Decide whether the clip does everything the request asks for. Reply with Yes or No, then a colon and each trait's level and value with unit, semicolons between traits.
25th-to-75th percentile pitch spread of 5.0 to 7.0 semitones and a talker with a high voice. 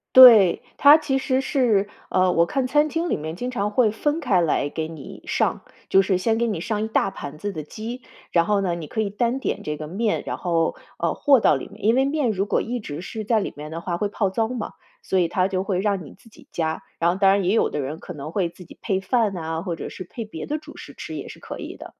Yes: wide, 5.6 semitones; high, 200 Hz